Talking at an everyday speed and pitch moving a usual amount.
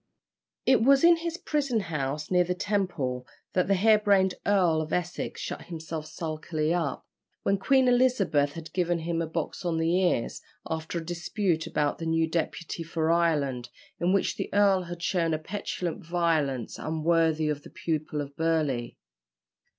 Yes: average, 165 wpm; average, 3.2 semitones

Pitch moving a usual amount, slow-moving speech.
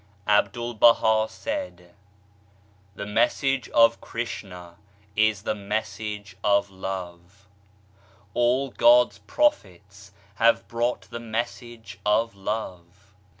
Yes: average, 3.0 semitones; slow, 95 wpm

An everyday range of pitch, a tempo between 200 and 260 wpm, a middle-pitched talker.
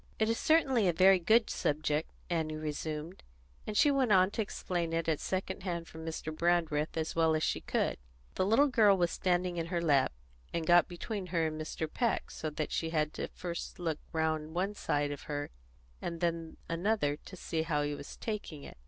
Yes: average, 3.2 semitones; fast, 205 wpm; medium, 170 Hz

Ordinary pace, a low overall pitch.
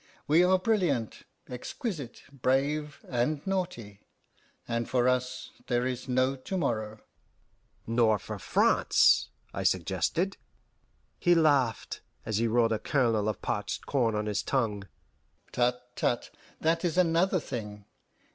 No: slow, 130 wpm; low, 125 Hz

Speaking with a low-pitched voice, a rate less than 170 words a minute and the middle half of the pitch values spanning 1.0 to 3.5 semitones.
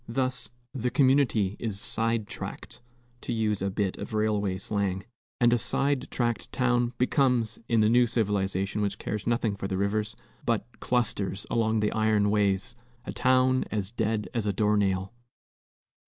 Yes: low, 110 Hz; average, 160 wpm; average, 3.0 semitones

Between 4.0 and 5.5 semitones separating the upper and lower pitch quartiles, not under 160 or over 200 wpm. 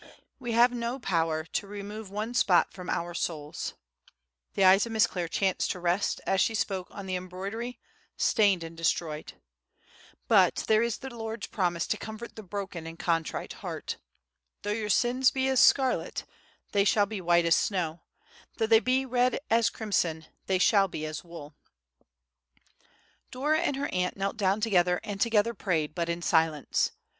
Yes: average, 4.6 semitones; average, 170 wpm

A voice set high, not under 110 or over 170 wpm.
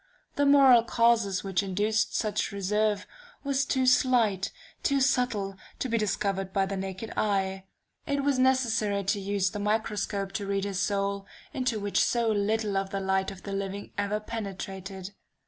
Yes: high, 205 Hz; average, 165 wpm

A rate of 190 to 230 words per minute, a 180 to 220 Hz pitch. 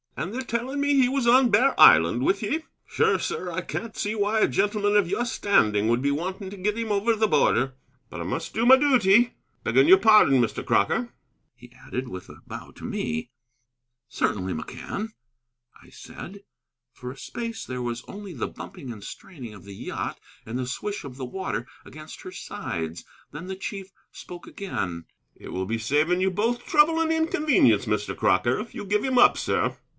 Yes: average, 195 wpm; high, 190 Hz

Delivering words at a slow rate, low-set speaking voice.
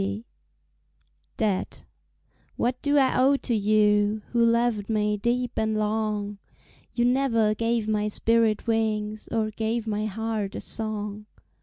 No: slow, 130 wpm; high, 220 Hz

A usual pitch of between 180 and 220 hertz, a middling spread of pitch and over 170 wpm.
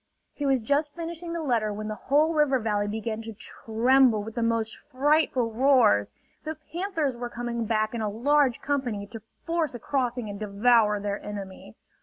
No: high, 235 Hz; average, 4.8 semitones; average, 180 wpm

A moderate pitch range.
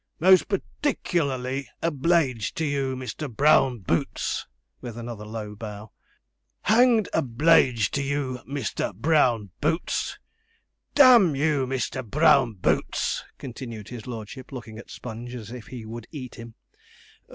Yes: average, 4.5 semitones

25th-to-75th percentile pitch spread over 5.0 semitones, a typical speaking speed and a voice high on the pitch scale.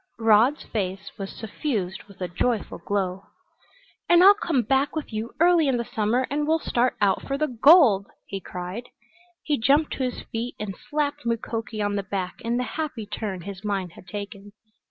Yes: wide, 5.5 semitones; average, 185 wpm; high, 225 Hz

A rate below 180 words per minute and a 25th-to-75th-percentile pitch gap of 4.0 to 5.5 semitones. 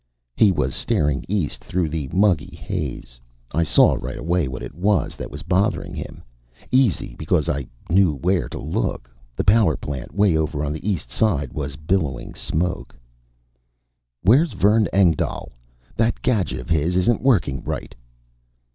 Yes: average, 155 wpm; average, 5.1 semitones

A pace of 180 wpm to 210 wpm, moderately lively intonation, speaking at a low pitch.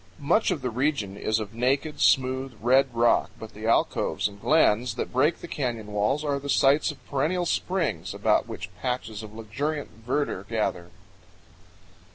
No: average, 165 wpm; average, 4.7 semitones; low, 125 Hz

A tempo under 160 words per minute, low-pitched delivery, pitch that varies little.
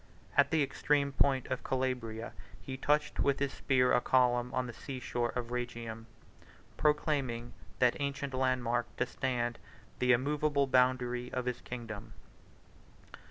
Yes: average, 150 wpm; low, 125 Hz; narrow, 2.2 semitones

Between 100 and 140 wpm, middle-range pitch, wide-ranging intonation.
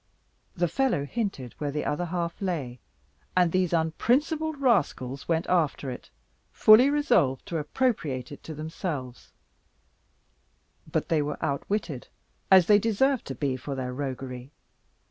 Yes: slow, 135 wpm; medium, 160 Hz; wide, 6.9 semitones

